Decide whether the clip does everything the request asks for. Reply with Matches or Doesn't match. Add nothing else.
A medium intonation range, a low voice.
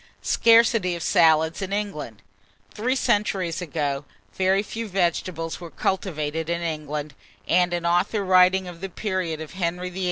Doesn't match